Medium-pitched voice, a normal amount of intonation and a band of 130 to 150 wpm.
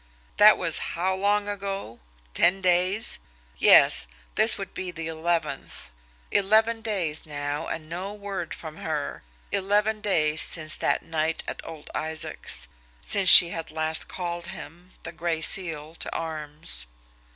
Yes: medium, 170 Hz; average, 3.6 semitones; average, 140 wpm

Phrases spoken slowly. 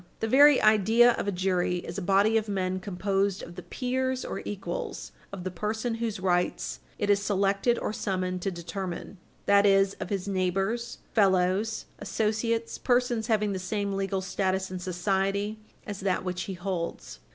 No: average, 170 wpm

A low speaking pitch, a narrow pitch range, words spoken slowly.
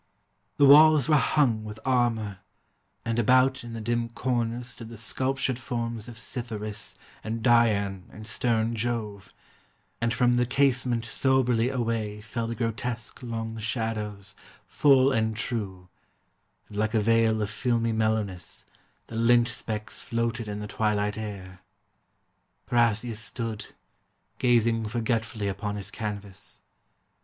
Yes: low, 115 Hz; narrow, 2.1 semitones; slow, 130 wpm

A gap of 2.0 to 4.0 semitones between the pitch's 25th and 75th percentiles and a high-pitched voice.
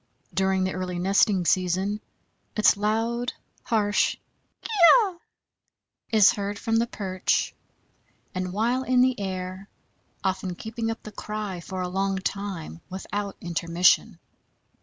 Yes: average, 2.7 semitones; high, 195 Hz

